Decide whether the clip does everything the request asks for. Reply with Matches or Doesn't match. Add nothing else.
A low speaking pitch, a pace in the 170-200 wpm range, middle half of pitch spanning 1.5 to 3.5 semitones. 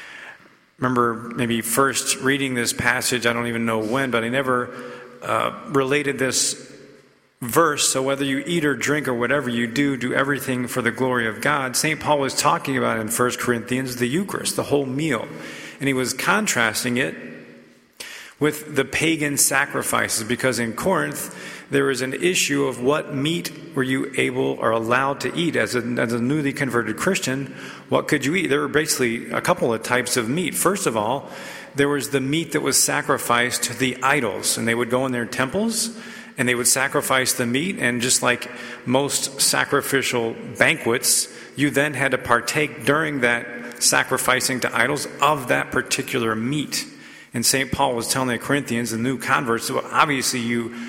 Matches